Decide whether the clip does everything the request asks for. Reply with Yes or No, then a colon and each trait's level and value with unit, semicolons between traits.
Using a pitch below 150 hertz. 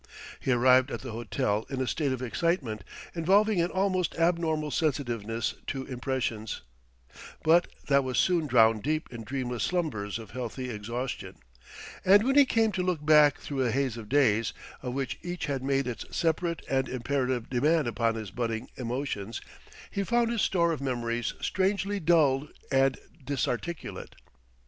Yes: low, 135 Hz